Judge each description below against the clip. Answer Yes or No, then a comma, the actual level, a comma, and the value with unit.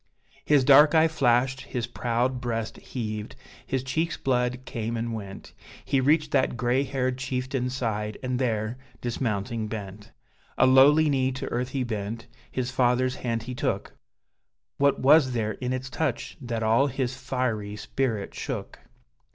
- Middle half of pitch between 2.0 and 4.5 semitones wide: Yes, narrow, 2.5 semitones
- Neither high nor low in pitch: No, low, 125 Hz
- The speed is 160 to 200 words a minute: No, average, 150 wpm